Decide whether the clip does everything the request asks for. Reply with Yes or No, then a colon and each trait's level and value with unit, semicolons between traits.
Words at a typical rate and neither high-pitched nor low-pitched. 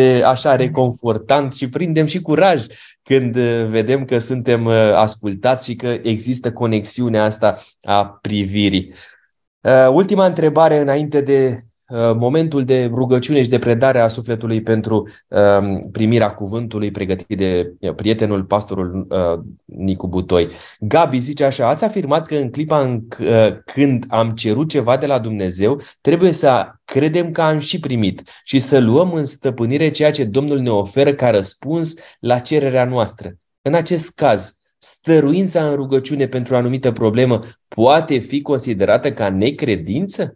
No: average, 145 wpm; low, 125 Hz